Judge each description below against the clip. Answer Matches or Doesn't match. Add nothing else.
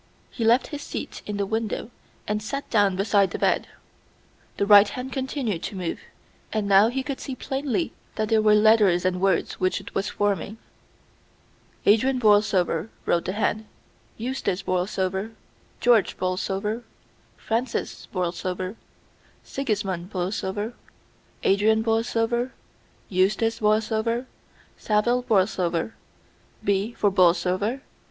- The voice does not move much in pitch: Doesn't match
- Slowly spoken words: Matches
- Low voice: Doesn't match